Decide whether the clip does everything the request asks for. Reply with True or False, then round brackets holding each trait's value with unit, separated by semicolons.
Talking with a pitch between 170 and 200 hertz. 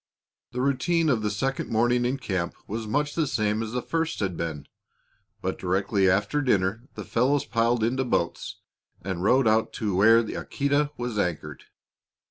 False (115 Hz)